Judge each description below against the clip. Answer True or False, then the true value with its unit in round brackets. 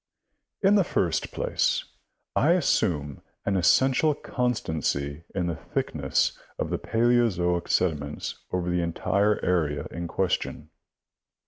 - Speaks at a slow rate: True (120 wpm)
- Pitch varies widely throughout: True (6.7 semitones)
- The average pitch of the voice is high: False (90 Hz)